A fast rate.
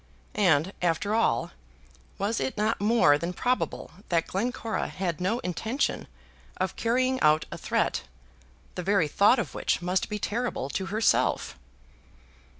No: average, 140 wpm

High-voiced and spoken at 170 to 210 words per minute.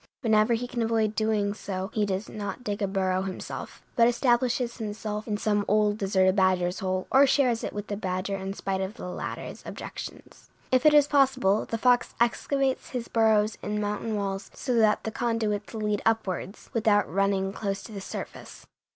Yes: high, 210 Hz; average, 185 wpm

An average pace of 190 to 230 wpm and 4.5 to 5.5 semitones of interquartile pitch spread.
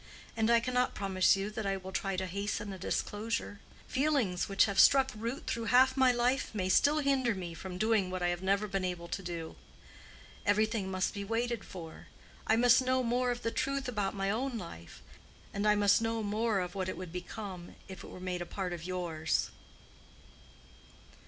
No: average, 195 wpm; average, 4.1 semitones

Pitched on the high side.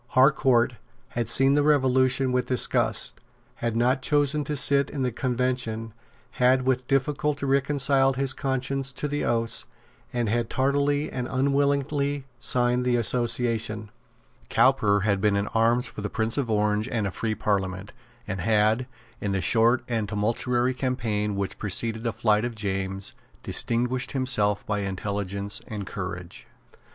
No: low, 120 Hz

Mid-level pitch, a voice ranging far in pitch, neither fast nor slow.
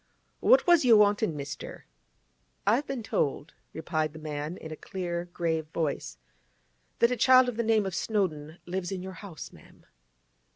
Yes: medium, 180 Hz; wide, 5.7 semitones; average, 170 wpm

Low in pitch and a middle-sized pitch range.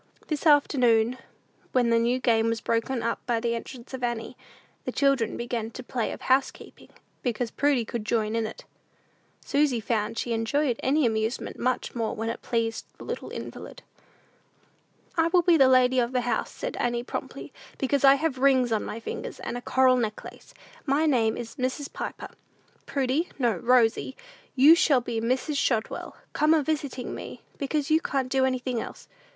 No: very high, 250 Hz; average, 3.1 semitones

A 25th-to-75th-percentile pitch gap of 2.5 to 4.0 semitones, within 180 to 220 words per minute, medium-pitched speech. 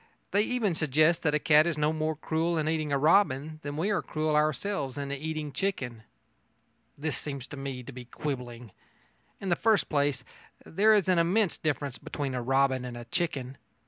Yes: average, 3.6 semitones; average, 185 wpm; medium, 150 Hz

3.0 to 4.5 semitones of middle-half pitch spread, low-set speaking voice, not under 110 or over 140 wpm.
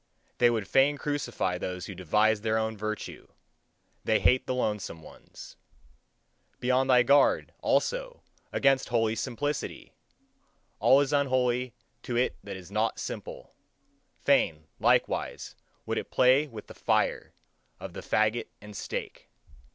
Yes: average, 3.8 semitones; low, 120 Hz; slow, 135 wpm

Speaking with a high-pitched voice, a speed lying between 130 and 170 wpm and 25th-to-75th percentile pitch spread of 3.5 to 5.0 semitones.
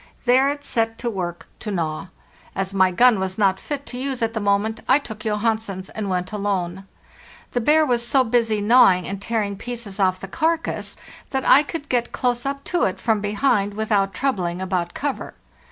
No: high, 220 Hz; average, 190 wpm; average, 4.4 semitones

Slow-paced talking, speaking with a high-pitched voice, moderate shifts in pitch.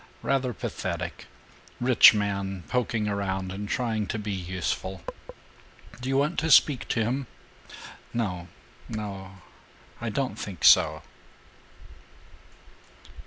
No: slow, 110 wpm; low, 105 Hz; average, 4.5 semitones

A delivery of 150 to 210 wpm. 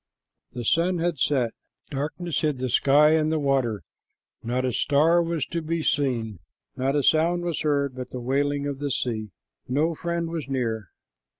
Yes: average, 175 wpm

